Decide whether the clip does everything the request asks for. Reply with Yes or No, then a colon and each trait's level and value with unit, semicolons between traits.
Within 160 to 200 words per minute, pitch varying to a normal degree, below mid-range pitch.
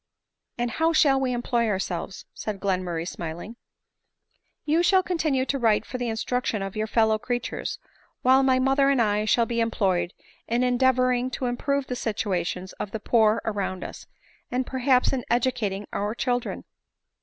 No: average, 170 wpm; average, 3.8 semitones; high, 240 Hz